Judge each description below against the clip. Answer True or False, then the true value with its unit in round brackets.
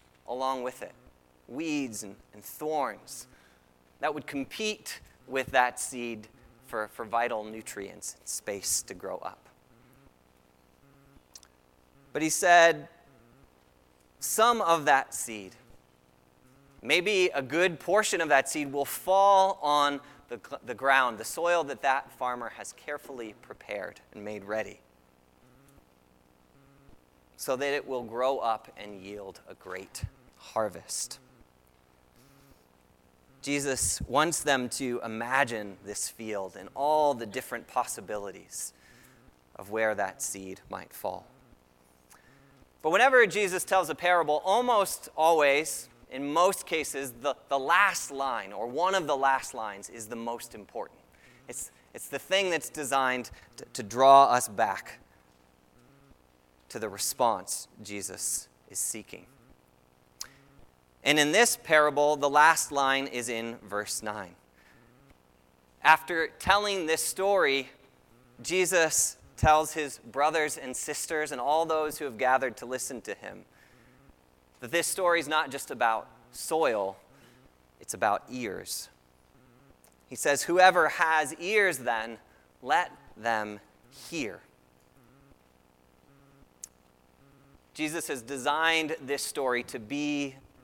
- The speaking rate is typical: False (120 wpm)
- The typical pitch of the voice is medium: False (120 Hz)